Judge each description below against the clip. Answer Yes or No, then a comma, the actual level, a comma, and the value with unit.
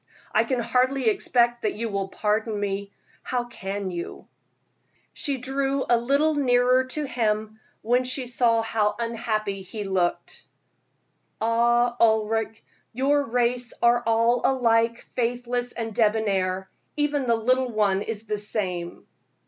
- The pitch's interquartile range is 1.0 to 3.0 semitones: Yes, average, 2.7 semitones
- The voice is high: Yes, high, 230 Hz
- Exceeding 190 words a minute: No, average, 140 wpm